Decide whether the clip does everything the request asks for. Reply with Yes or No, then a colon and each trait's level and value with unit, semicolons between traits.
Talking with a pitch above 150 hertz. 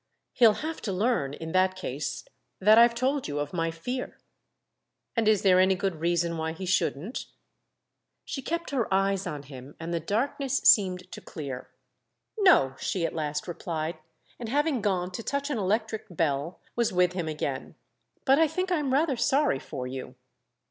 Yes: high, 190 Hz